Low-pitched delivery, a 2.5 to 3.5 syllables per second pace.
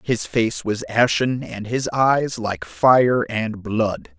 Yes: low, 110 Hz; 3.0 syllables/s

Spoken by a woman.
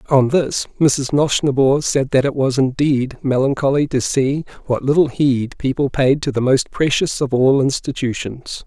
No: male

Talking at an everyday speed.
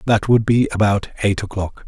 Yes: average, 190 wpm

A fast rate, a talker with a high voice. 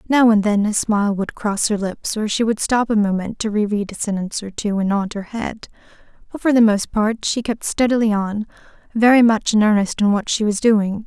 Yes: fast, 235 wpm; high, 215 Hz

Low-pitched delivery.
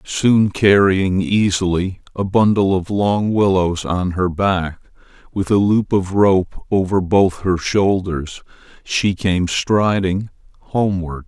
Yes: very low, 95 Hz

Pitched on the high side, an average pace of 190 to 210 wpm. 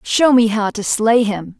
No: high, 220 Hz; fast, 225 wpm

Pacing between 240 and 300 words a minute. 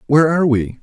No: fast, 220 wpm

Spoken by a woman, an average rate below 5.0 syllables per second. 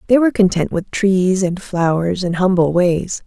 Yes: female; 4.5 syllables/s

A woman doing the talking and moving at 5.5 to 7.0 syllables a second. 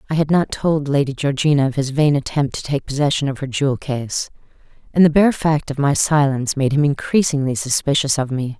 Yes: female; 5.7 syllables/s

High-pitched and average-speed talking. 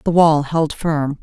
No: medium, 155 Hz; average, 195 wpm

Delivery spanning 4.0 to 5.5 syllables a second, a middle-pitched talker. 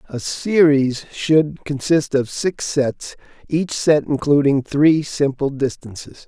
No: 3.5 syllables/s; medium, 145 Hz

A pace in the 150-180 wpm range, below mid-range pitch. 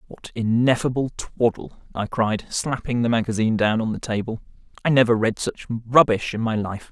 Yes: average, 175 wpm; low, 115 Hz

